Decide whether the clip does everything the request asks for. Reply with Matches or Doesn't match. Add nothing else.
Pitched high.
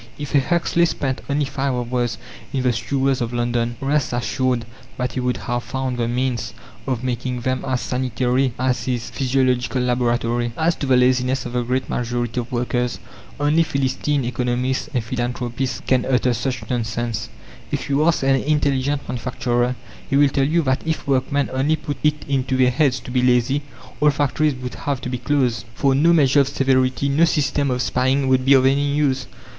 Doesn't match